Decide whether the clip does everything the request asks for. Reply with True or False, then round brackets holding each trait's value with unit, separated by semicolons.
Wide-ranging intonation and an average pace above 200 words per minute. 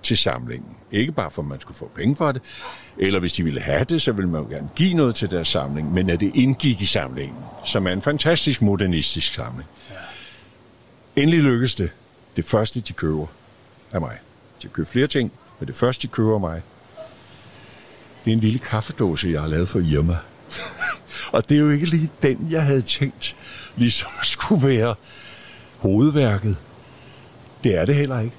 False (6.8 semitones; 190 wpm)